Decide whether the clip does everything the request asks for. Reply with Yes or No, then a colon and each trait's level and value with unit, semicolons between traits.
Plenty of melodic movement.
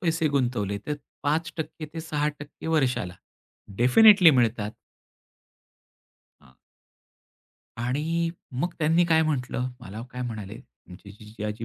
Yes: wide, 6.0 semitones